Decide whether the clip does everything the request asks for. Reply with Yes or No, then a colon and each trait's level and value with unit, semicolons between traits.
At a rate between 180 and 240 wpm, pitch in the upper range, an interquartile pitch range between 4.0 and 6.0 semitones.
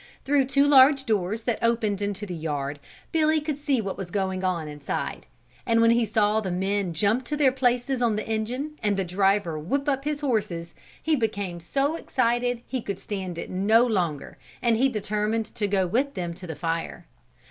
Yes: average, 195 wpm; high, 215 Hz; wide, 5.4 semitones